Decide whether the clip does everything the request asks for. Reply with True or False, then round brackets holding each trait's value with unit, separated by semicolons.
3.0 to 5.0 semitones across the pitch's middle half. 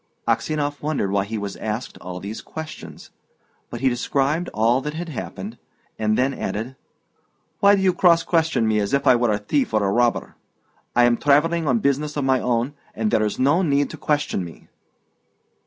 False (5.5 semitones)